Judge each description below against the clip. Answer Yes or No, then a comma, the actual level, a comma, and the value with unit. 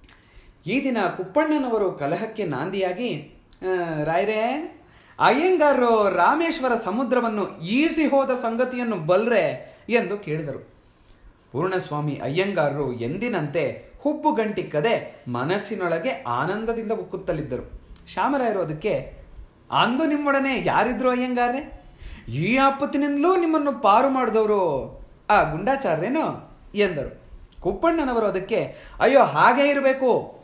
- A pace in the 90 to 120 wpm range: No, average, 80 wpm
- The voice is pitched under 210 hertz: No, high, 225 Hz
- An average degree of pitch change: No, wide, 7.1 semitones